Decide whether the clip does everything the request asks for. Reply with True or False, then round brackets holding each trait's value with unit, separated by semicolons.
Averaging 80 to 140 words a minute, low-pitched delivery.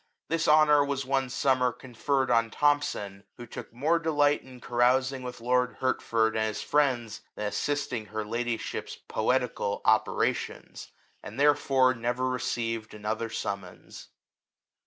True (135 wpm; 125 Hz)